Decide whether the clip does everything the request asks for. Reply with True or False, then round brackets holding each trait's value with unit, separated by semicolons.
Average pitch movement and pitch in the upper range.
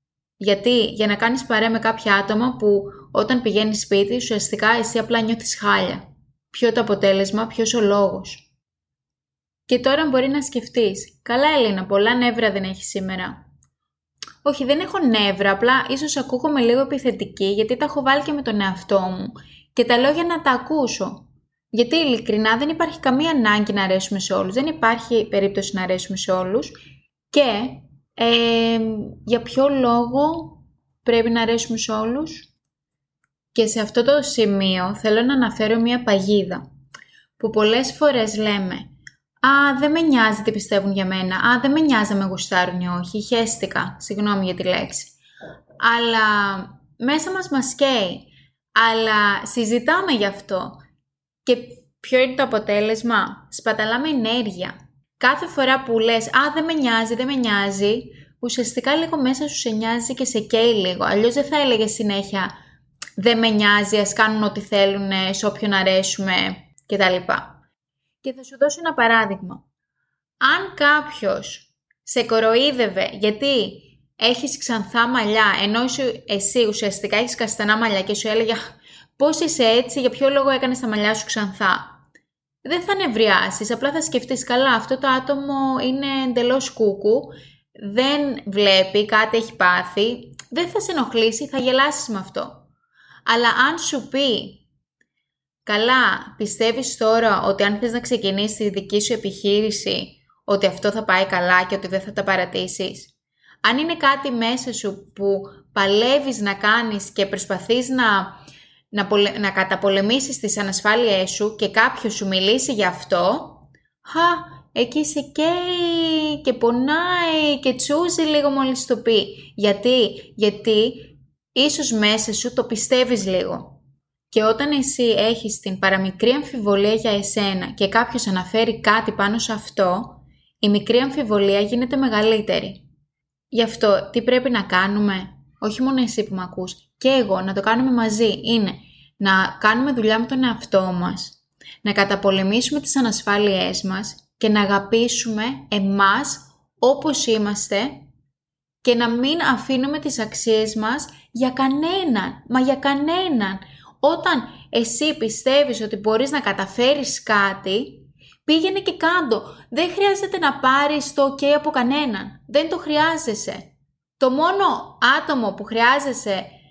True (4.7 semitones; 225 Hz)